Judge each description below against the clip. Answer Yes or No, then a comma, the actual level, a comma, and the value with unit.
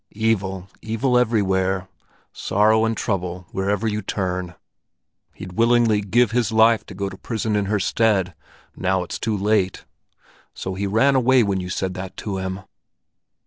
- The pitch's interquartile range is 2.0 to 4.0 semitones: Yes, average, 2.9 semitones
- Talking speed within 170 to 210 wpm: No, average, 155 wpm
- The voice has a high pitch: No, low, 100 Hz